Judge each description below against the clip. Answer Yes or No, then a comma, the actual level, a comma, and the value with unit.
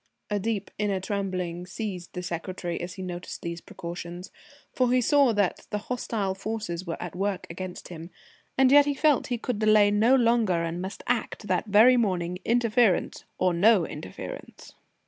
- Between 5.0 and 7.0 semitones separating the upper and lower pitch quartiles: No, average, 4.3 semitones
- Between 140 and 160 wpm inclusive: No, average, 170 wpm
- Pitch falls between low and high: No, high, 200 Hz